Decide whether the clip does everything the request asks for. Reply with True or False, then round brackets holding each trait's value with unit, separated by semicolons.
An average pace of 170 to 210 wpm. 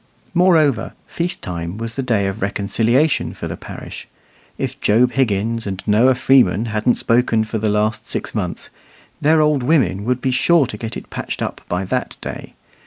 True (175 wpm)